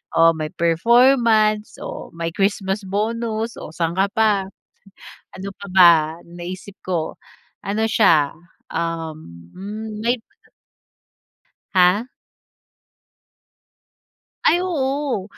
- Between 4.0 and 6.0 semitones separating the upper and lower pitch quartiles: Yes, average, 4.5 semitones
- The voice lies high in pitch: Yes, high, 200 Hz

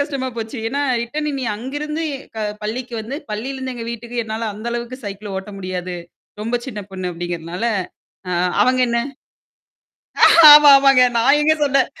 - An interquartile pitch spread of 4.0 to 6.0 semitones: Yes, average, 4.4 semitones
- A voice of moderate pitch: No, high, 235 Hz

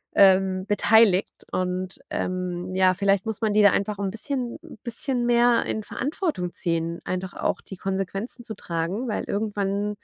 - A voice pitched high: Yes, high, 200 Hz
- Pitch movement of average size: Yes, average, 3.2 semitones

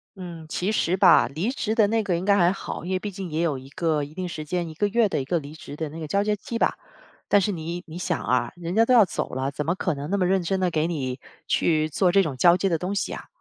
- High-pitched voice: No, medium, 175 Hz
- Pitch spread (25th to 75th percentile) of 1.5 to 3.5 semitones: No, average, 3.9 semitones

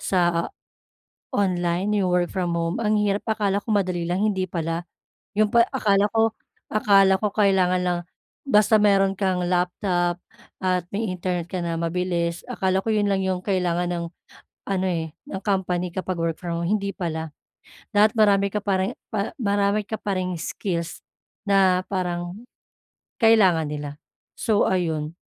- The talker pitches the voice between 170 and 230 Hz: Yes, medium, 185 Hz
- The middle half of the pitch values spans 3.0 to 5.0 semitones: No, narrow, 2.5 semitones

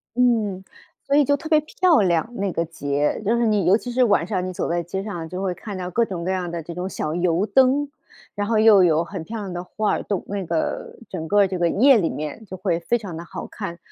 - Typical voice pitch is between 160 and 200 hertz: Yes, high, 190 Hz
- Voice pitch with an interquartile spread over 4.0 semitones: Yes, average, 4.4 semitones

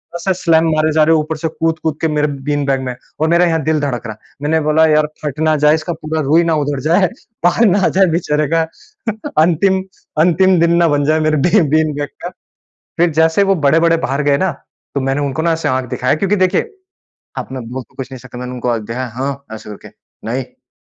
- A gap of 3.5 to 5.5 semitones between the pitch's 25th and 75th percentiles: No, average, 3.0 semitones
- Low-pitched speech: No, medium, 155 Hz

